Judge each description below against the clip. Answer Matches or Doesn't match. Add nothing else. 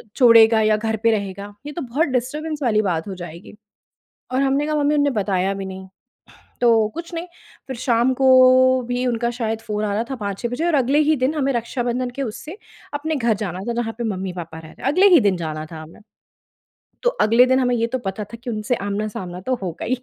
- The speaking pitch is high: Matches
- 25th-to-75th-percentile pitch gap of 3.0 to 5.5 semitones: Matches